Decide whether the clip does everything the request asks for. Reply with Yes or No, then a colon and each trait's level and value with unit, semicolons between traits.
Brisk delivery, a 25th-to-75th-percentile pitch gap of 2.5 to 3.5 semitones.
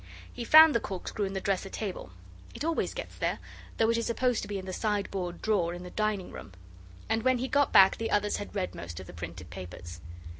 No: fast, 230 wpm; average, 4.3 semitones